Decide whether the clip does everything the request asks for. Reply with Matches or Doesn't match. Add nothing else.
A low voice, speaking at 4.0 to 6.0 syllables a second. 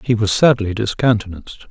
Matches